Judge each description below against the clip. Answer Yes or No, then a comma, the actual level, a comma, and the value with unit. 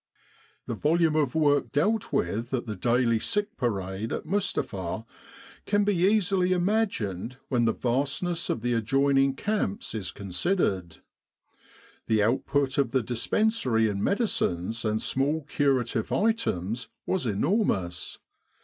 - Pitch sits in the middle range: No, low, 130 Hz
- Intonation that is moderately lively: No, wide, 8.2 semitones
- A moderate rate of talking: No, slow, 125 wpm